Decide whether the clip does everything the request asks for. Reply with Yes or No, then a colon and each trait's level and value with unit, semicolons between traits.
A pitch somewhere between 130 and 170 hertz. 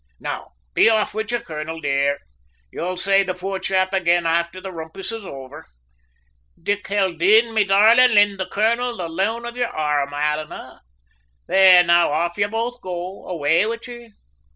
No: high, 190 Hz